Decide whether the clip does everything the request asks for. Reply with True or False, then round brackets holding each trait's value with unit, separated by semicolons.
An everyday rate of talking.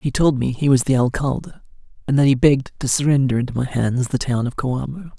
False (230 wpm)